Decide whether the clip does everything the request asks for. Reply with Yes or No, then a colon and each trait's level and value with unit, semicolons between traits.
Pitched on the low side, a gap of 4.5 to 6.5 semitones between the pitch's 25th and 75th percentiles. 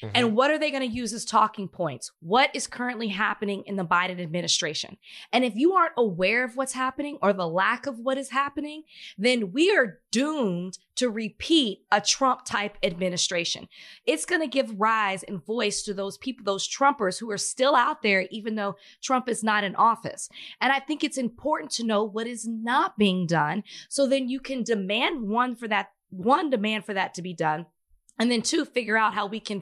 No: high, 225 Hz; average, 4.8 semitones